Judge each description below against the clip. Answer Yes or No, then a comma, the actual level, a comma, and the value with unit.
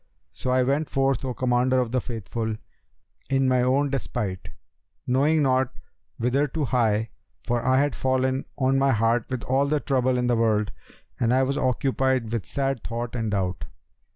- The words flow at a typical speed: Yes, average, 165 wpm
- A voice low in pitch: Yes, low, 130 Hz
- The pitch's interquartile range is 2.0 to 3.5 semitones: Yes, narrow, 2.5 semitones